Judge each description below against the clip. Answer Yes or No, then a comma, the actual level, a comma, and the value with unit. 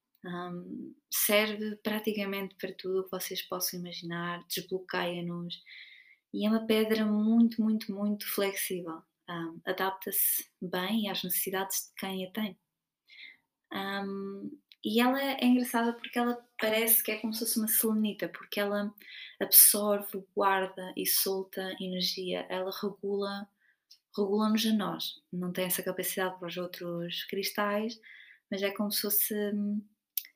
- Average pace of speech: Yes, average, 135 wpm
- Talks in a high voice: Yes, high, 200 Hz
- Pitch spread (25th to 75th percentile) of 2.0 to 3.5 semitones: Yes, average, 2.8 semitones